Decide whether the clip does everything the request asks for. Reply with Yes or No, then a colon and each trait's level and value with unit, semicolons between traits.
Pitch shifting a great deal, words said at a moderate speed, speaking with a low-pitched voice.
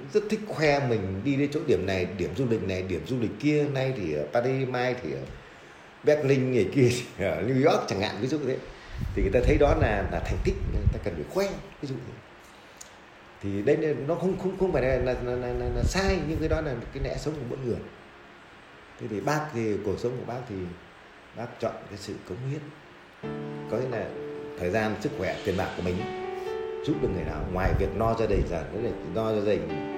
Yes: wide, 7.5 semitones; average, 240 wpm; low, 125 Hz